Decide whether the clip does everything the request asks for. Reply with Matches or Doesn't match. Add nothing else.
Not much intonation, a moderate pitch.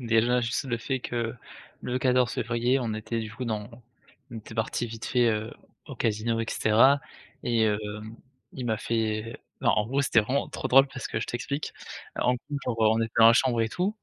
Doesn't match